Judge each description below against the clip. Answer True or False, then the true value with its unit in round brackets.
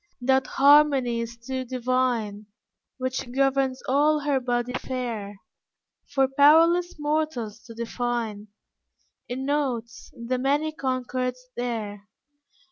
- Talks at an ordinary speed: False (105 wpm)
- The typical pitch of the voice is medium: False (255 Hz)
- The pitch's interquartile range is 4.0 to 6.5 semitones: False (2.6 semitones)